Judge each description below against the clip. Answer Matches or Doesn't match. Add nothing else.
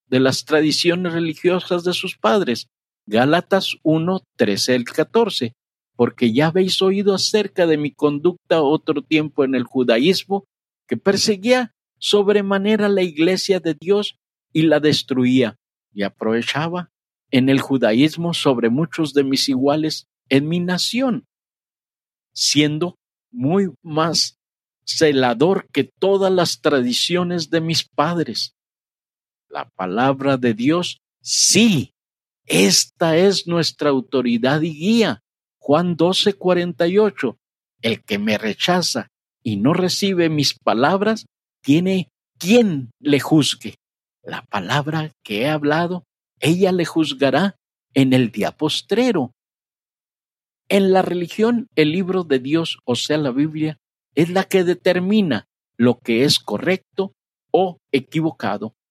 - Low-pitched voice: Doesn't match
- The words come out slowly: Matches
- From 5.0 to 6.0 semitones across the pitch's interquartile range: Matches